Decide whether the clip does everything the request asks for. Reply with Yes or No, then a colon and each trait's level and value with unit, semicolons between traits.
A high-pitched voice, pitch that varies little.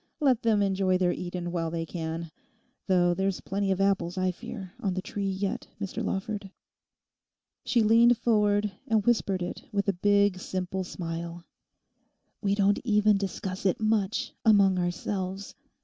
Yes: high, 195 Hz; narrow, 2.2 semitones